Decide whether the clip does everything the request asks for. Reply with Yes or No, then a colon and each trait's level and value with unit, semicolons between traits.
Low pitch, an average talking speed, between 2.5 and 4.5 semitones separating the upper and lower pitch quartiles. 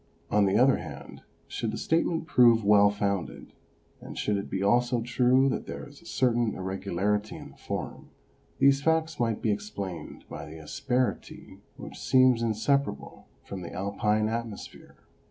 Yes: low, 110 Hz; average, 155 wpm; average, 4.2 semitones